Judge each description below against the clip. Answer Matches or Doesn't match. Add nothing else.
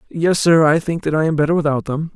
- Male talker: Matches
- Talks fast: Matches